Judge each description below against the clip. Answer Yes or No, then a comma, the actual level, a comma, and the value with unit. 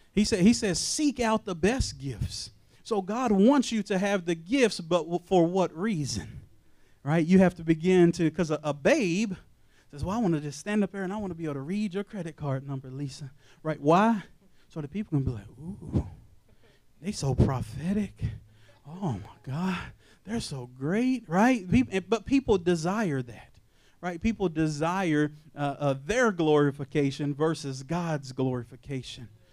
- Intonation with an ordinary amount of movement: No, wide, 6.6 semitones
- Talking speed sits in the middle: Yes, average, 175 wpm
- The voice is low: No, medium, 165 Hz